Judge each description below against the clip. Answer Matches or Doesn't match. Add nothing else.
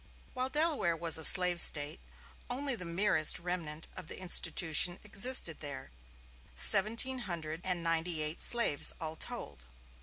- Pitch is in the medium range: Matches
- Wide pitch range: Doesn't match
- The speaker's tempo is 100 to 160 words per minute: Matches